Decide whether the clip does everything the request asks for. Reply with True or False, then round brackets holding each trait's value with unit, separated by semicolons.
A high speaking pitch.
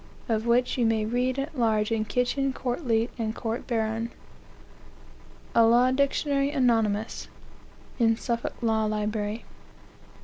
True (230 Hz)